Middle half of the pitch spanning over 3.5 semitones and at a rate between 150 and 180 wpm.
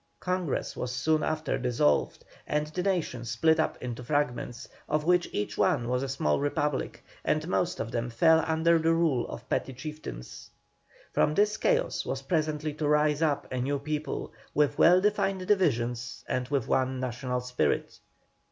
Yes: average, 4.5 semitones; average, 165 wpm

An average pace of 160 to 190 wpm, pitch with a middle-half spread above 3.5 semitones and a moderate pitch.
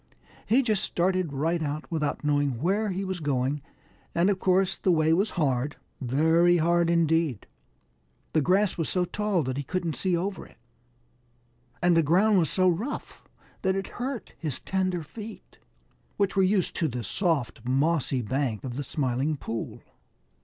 Yes: average, 165 wpm; average, 4.7 semitones; medium, 170 Hz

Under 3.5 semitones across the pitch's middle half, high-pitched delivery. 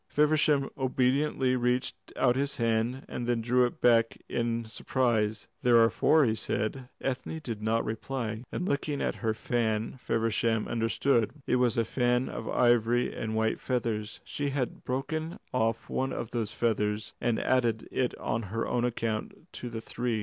No: narrow, 2.5 semitones; low, 120 Hz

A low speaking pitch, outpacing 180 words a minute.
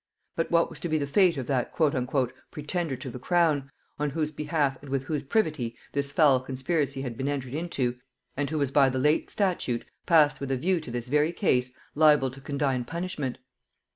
No: medium, 145 Hz; average, 200 wpm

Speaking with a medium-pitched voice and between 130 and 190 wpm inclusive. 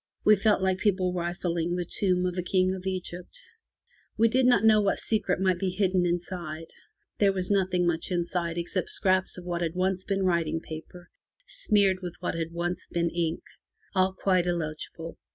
Yes: medium, 180 Hz; average, 180 wpm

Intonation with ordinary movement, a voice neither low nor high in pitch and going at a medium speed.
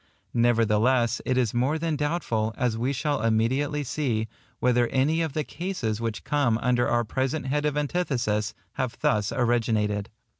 No: average, 4.4 semitones; low, 125 Hz; average, 155 wpm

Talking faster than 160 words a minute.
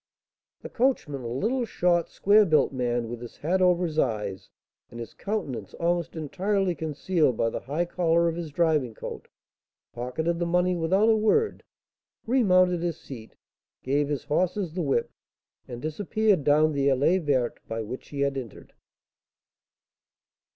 No: average, 155 wpm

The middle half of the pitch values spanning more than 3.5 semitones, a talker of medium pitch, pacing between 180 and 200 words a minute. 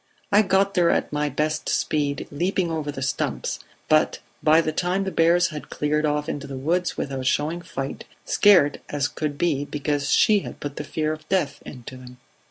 No: average, 3.2 semitones; medium, 150 Hz; average, 190 wpm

